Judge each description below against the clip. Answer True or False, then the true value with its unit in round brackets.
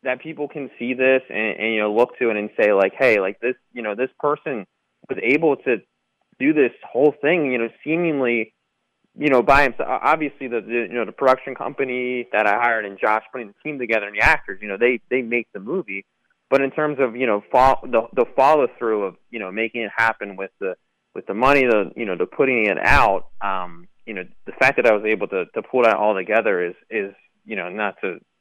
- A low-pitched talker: True (120 Hz)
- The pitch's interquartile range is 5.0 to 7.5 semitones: False (3.6 semitones)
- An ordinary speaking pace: False (230 wpm)